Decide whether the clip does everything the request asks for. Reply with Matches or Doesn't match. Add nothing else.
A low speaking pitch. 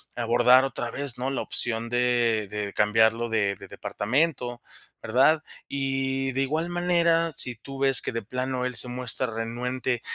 Matches